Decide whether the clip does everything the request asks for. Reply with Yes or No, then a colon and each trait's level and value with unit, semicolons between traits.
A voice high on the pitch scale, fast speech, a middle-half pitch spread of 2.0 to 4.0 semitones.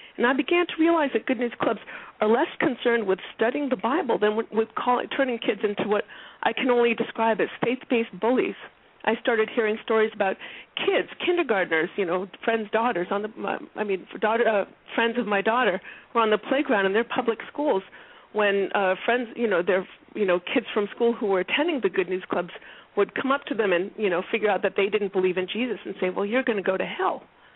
Yes: high, 225 Hz; fast, 225 wpm; average, 3.6 semitones